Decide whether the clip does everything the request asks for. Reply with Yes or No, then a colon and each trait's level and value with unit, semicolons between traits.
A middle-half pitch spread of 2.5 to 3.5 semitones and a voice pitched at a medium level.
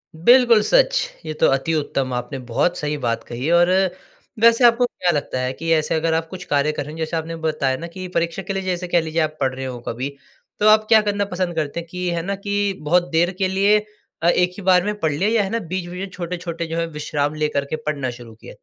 No: average, 3.9 semitones; medium, 170 Hz